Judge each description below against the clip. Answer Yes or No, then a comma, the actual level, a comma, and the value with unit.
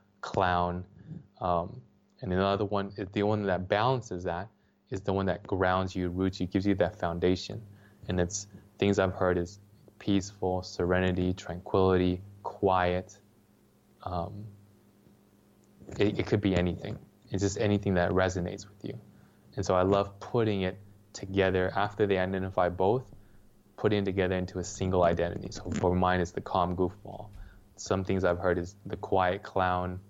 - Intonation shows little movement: Yes, narrow, 1.9 semitones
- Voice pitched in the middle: No, very low, 95 Hz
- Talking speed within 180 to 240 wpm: No, average, 155 wpm